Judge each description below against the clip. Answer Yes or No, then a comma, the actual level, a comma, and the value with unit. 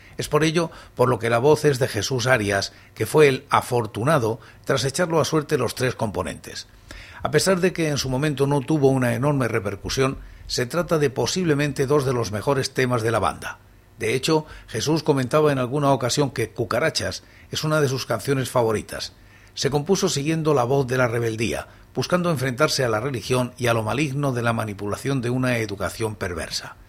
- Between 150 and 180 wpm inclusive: No, fast, 190 wpm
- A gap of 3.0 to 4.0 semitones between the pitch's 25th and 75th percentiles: No, average, 4.7 semitones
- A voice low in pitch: Yes, low, 130 Hz